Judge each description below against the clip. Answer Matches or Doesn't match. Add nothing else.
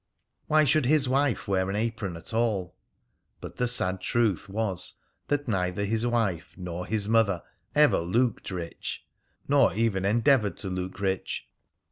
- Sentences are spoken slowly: Doesn't match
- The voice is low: Matches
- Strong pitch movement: Doesn't match